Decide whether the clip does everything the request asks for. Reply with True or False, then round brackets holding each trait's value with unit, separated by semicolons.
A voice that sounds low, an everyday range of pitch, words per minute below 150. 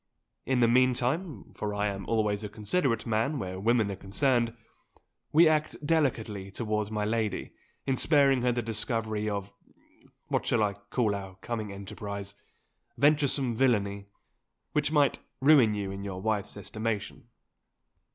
True (110 Hz; 4.1 semitones; 140 wpm)